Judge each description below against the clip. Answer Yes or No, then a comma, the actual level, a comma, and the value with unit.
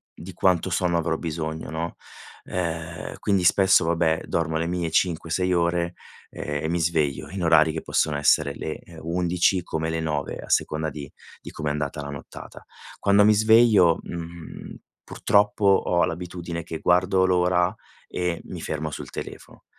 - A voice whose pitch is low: Yes, very low, 85 Hz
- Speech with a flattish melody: Yes, narrow, 2.2 semitones